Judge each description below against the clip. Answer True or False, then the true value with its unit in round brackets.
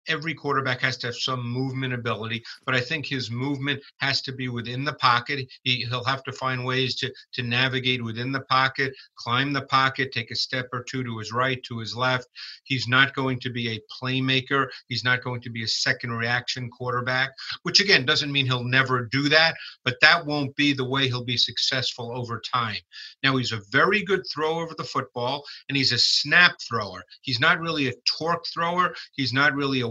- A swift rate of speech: True (210 wpm)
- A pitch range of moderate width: False (1.9 semitones)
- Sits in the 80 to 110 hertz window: False (130 Hz)